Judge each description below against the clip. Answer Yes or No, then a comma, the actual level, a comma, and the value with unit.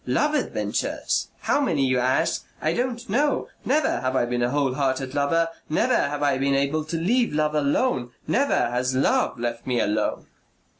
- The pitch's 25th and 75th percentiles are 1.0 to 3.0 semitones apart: No, average, 4.6 semitones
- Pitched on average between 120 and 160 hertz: Yes, medium, 140 Hz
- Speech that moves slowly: No, average, 180 wpm